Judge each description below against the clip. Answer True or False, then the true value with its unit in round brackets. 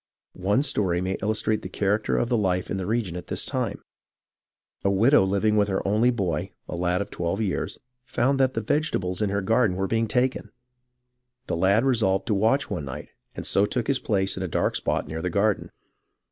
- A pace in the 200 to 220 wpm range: True (205 wpm)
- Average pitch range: True (3.4 semitones)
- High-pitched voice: False (100 Hz)